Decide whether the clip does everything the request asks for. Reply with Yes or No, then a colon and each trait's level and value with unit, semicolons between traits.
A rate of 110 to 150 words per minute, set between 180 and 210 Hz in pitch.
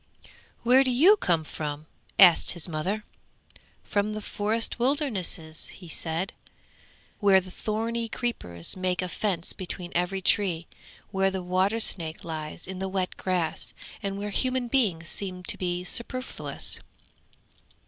Yes: average, 140 wpm; high, 190 Hz